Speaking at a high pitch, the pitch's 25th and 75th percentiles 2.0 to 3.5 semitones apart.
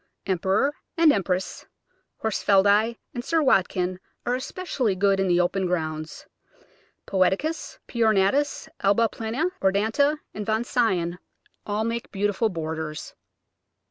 No: high, 205 Hz; average, 4.1 semitones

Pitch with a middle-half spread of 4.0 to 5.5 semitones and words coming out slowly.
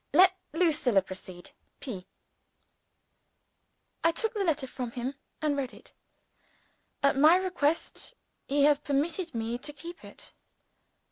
Yes: average, 5.0 semitones; slow, 125 wpm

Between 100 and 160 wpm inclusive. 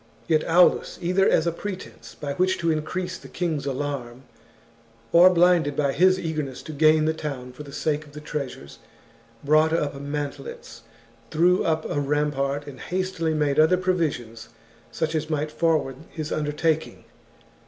Yes: average, 155 wpm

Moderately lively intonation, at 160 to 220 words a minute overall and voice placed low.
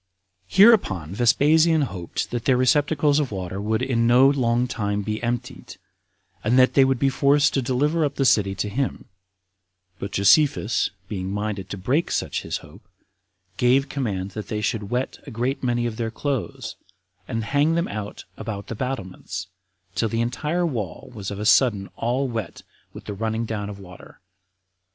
Yes: average, 4.8 semitones; average, 180 wpm; low, 120 Hz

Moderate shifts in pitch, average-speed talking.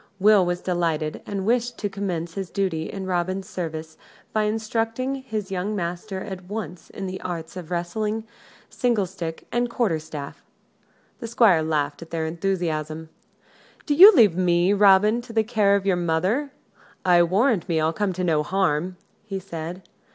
Yes: average, 4.0 semitones; average, 165 wpm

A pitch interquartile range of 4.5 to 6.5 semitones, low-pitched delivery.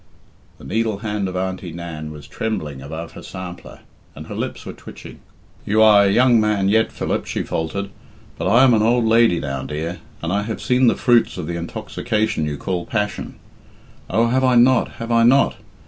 Yes: average, 5.1 semitones; low, 105 Hz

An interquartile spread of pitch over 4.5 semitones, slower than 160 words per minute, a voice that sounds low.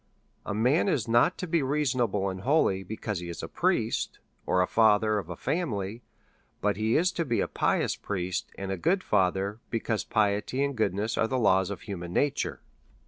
No: average, 5.1 semitones; average, 200 wpm; low, 110 Hz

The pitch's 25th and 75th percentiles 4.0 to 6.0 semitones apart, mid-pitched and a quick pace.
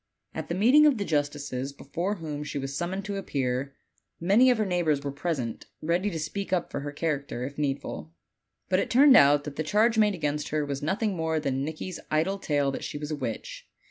Yes: average, 5.2 semitones; medium, 155 Hz; fast, 220 wpm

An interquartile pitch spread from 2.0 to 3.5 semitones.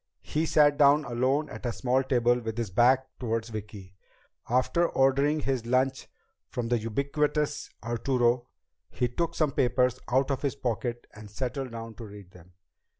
Yes: average, 2.9 semitones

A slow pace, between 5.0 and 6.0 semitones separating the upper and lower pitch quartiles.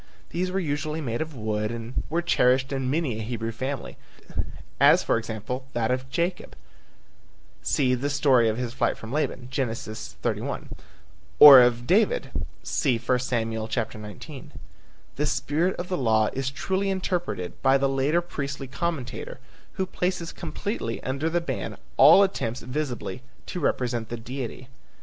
No: average, 150 wpm; average, 5.3 semitones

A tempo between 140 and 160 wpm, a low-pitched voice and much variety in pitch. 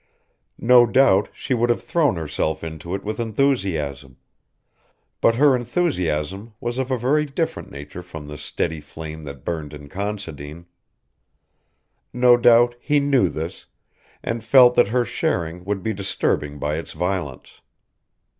Yes: average, 145 wpm; low, 100 Hz; wide, 7.6 semitones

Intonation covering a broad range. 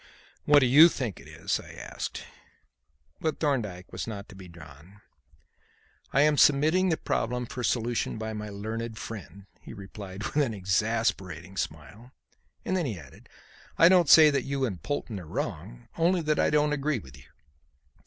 Yes: wide, 7.0 semitones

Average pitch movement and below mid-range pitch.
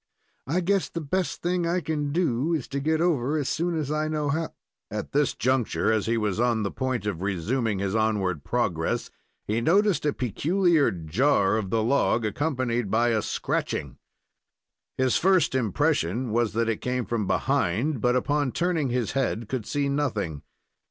No: wide, 5.8 semitones; low, 125 Hz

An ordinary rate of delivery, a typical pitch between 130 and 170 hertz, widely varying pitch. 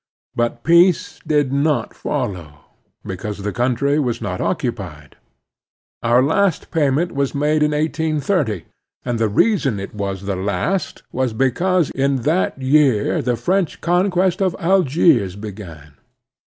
No: slow, 130 wpm; low, 135 Hz; wide, 7.5 semitones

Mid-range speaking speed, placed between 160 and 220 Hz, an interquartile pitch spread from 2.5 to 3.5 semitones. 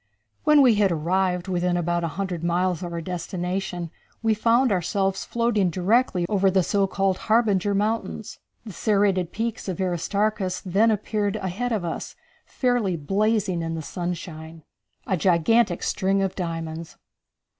Yes: average, 145 wpm; high, 190 Hz; average, 3.2 semitones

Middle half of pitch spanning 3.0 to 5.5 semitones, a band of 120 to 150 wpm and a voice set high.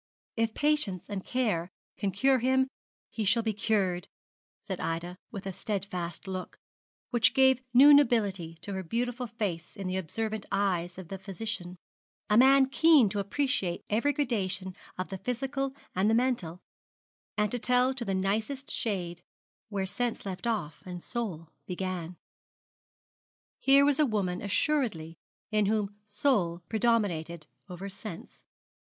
Yes: average, 4.9 semitones; average, 145 wpm; high, 205 Hz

